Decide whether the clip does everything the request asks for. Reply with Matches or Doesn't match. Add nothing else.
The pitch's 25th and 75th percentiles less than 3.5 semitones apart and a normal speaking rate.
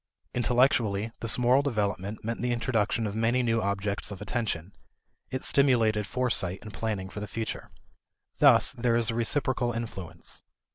Matches